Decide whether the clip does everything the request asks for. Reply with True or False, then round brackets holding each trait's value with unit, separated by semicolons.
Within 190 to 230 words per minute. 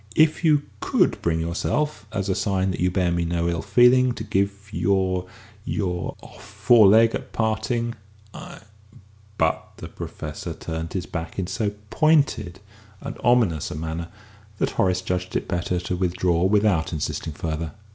False (165 wpm)